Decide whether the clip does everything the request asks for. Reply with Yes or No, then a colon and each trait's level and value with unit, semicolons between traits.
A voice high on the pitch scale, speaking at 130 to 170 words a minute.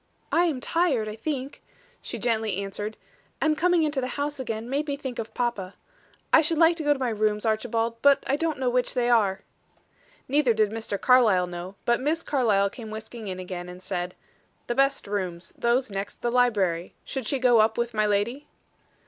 No: high, 235 Hz; average, 200 wpm